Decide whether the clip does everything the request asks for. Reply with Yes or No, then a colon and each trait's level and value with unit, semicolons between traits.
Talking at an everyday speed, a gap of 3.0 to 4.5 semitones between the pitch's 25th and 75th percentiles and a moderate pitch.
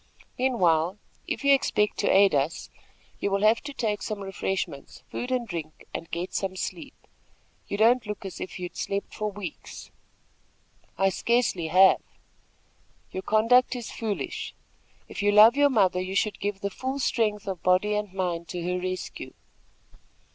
No: average, 165 wpm; average, 3.4 semitones; high, 200 Hz